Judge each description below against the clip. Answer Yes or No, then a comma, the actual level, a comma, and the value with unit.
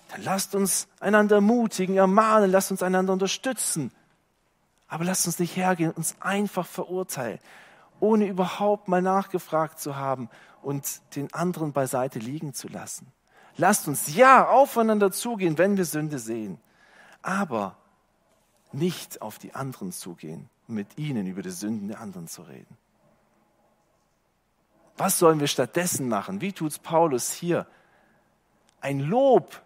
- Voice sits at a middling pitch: Yes, medium, 180 Hz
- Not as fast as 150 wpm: Yes, average, 140 wpm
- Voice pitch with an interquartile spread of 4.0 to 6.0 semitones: Yes, average, 5.0 semitones